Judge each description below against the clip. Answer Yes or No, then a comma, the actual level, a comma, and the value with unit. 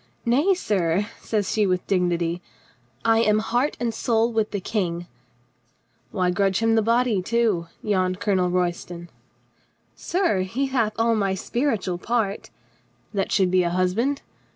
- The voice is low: No, high, 205 Hz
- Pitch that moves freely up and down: No, average, 4.1 semitones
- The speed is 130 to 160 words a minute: Yes, average, 155 wpm